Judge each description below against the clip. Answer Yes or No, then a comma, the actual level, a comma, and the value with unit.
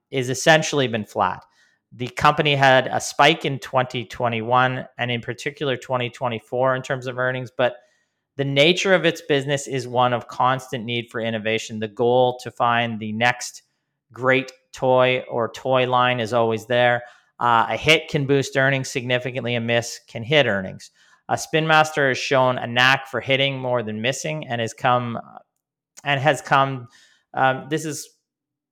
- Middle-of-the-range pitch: No, low, 130 Hz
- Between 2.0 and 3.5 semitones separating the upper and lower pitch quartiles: Yes, narrow, 2.6 semitones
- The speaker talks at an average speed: Yes, average, 165 wpm